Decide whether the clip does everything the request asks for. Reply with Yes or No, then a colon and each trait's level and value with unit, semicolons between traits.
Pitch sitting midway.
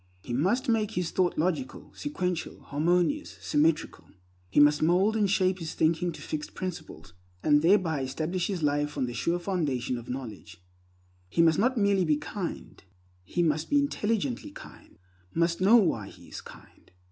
Yes: medium, 170 Hz